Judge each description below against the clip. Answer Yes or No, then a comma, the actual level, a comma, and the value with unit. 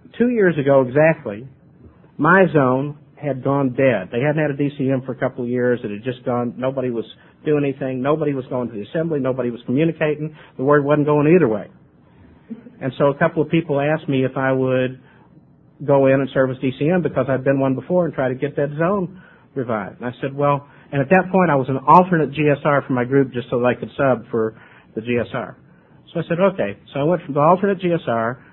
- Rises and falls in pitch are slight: No, average, 3.0 semitones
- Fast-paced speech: Yes, fast, 225 wpm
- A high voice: No, medium, 140 Hz